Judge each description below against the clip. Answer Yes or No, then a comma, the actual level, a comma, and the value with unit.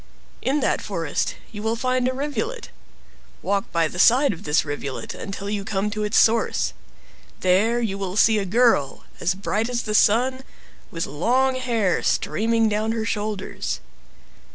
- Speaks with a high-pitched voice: Yes, high, 215 Hz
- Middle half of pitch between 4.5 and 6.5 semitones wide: No, average, 3.6 semitones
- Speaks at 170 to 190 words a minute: No, average, 160 wpm